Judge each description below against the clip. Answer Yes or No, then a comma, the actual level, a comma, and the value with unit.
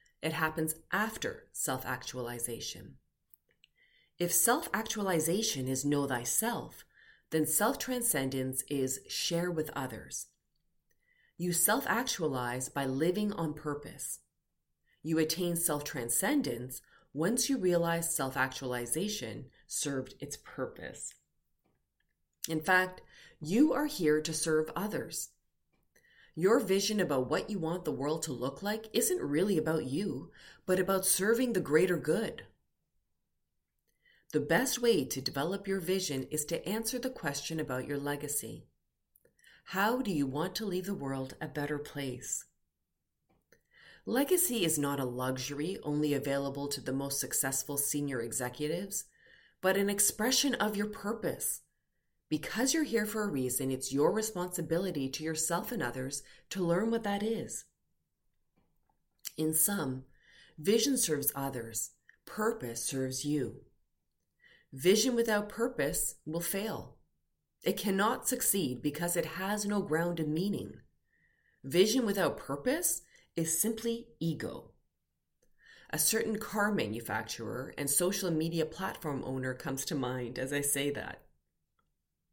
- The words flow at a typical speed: No, slow, 125 wpm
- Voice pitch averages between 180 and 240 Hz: No, medium, 155 Hz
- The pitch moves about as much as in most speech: No, wide, 7.0 semitones